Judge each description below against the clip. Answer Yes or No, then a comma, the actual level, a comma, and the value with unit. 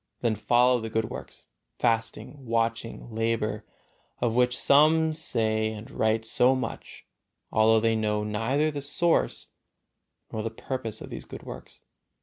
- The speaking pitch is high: No, low, 115 Hz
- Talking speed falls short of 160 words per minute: Yes, average, 140 wpm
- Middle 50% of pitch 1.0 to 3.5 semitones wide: Yes, average, 2.7 semitones